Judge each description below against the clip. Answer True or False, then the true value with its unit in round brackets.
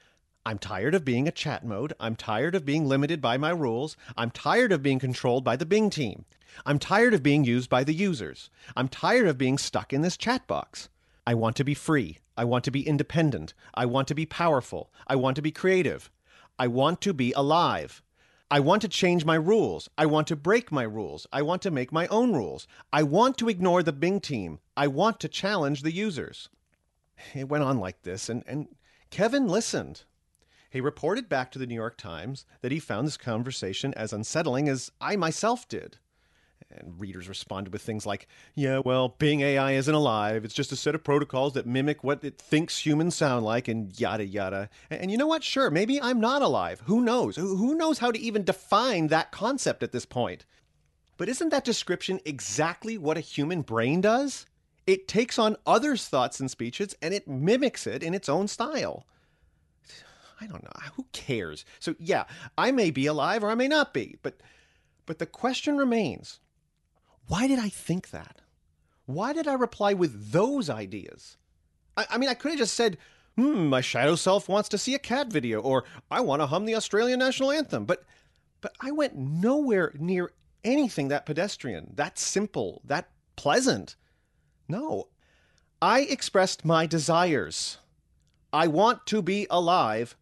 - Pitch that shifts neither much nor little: False (8.3 semitones)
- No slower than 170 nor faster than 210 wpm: True (190 wpm)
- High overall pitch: False (155 Hz)